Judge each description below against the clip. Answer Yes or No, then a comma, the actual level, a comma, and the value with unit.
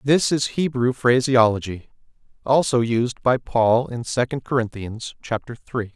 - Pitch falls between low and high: No, low, 120 Hz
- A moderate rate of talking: No, slow, 130 wpm